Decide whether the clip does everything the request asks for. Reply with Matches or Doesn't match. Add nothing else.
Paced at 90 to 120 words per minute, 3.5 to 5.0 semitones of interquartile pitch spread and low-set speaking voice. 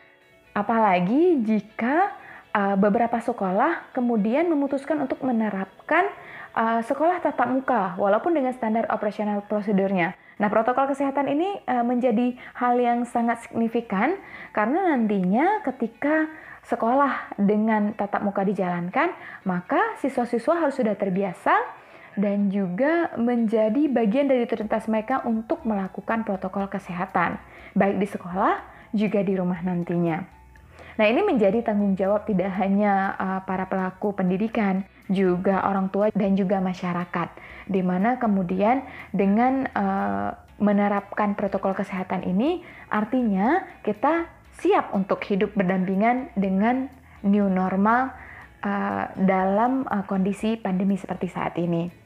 Doesn't match